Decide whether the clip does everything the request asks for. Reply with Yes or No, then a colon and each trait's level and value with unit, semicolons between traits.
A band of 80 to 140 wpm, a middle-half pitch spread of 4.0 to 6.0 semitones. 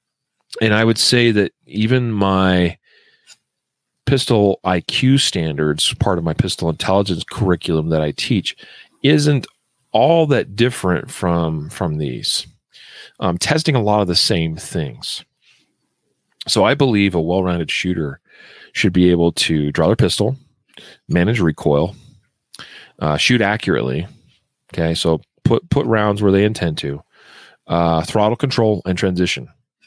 Yes: slow, 135 wpm; wide, 5.5 semitones